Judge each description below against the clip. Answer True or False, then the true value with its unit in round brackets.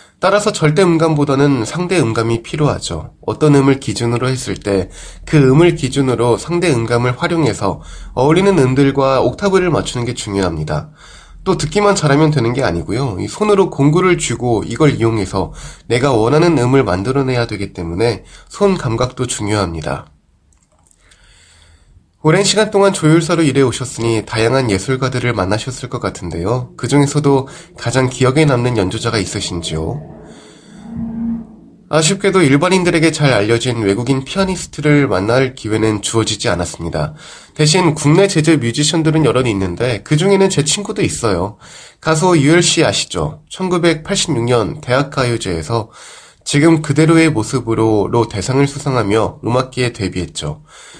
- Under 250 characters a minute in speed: False (330 characters per minute)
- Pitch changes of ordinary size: False (6.4 semitones)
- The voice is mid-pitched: False (130 Hz)